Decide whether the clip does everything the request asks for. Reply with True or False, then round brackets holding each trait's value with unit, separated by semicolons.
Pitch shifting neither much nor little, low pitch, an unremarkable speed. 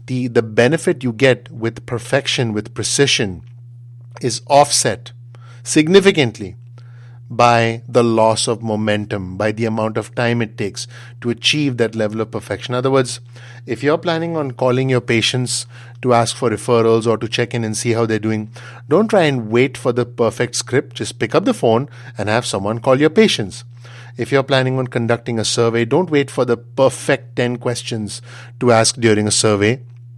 False (1.7 semitones; 120 Hz; 180 wpm)